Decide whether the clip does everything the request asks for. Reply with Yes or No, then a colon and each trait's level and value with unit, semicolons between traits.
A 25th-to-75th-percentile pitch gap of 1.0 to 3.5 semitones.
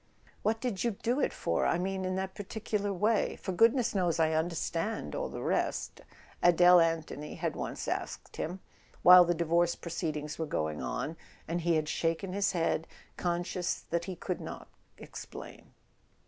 Yes: average, 2.9 semitones